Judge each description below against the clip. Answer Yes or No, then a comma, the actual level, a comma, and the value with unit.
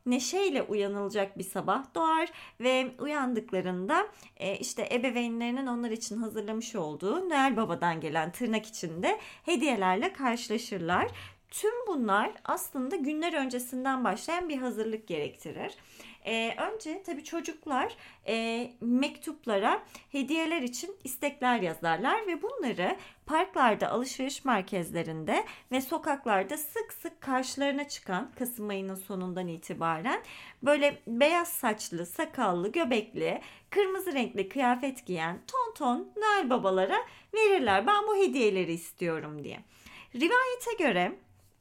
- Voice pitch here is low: No, very high, 250 Hz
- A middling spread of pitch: No, wide, 8.1 semitones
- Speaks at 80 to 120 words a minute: Yes, average, 110 wpm